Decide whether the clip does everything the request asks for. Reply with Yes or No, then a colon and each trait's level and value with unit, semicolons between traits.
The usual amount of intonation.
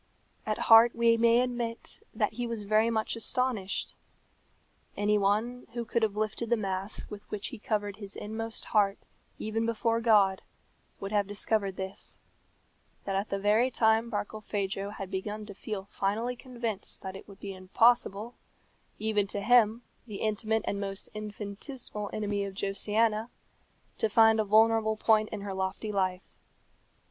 No: narrow, 2.2 semitones